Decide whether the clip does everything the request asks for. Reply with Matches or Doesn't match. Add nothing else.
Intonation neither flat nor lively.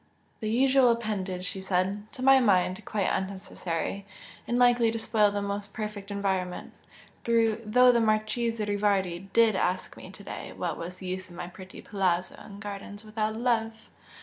Matches